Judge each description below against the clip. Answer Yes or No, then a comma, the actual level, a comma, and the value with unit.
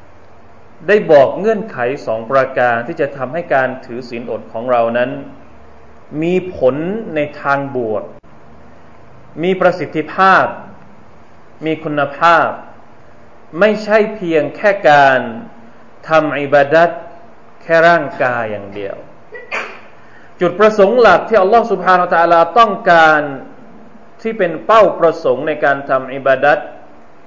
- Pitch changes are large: Yes, wide, 6.6 semitones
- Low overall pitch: No, medium, 155 Hz